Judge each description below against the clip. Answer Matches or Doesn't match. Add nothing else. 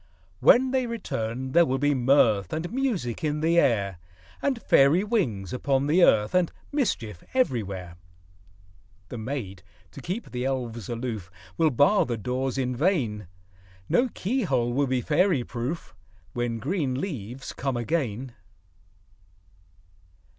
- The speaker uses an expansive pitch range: Matches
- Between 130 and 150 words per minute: Matches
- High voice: Doesn't match